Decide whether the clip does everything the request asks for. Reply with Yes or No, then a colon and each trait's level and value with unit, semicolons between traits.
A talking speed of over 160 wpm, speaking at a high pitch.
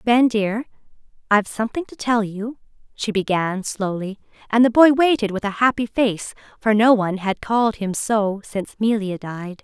Yes: average, 175 wpm; high, 215 Hz